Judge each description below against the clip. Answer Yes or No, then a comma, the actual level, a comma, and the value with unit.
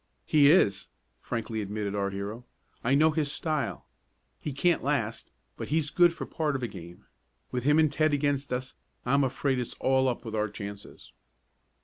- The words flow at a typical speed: Yes, average, 175 wpm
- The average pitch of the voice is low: Yes, low, 130 Hz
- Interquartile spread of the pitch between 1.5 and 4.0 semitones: No, wide, 5.5 semitones